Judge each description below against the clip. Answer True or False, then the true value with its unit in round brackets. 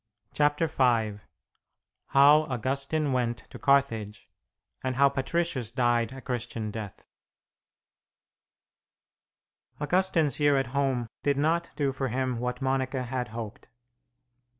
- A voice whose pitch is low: True (130 Hz)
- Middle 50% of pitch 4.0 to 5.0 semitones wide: False (3.0 semitones)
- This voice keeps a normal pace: False (110 wpm)